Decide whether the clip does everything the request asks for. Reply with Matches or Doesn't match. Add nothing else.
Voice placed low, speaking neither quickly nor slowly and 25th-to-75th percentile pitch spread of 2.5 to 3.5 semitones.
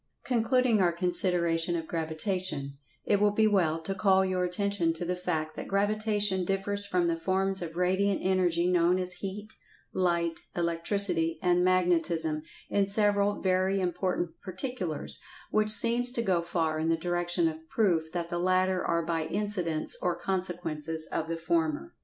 Doesn't match